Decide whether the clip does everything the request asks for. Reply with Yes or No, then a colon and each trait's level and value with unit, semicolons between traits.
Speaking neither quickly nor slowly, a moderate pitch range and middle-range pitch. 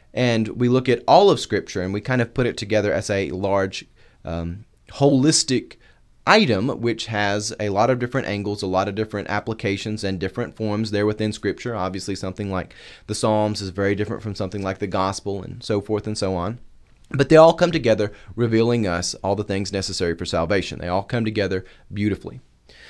No: average, 195 wpm; average, 3.0 semitones; low, 105 Hz